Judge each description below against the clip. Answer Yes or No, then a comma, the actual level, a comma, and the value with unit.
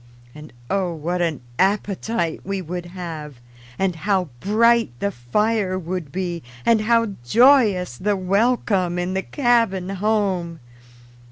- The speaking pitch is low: No, high, 190 Hz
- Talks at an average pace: No, slow, 125 wpm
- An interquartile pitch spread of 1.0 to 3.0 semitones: No, average, 3.4 semitones